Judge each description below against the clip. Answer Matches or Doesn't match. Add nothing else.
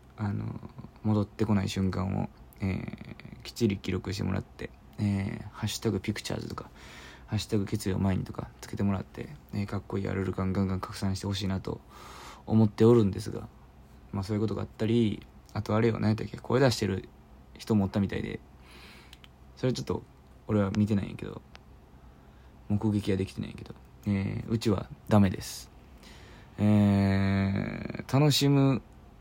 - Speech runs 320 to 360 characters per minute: Matches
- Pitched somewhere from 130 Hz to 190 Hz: Doesn't match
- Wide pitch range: Doesn't match